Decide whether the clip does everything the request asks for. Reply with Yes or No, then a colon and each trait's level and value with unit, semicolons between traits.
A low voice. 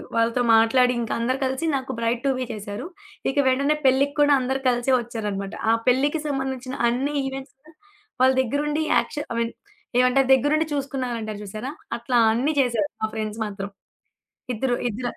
No: very high, 255 Hz